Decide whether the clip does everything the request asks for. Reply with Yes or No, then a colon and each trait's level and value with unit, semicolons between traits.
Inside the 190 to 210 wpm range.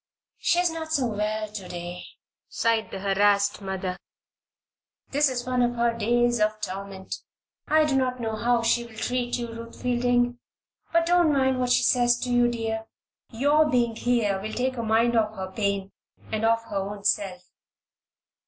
No: average, 175 wpm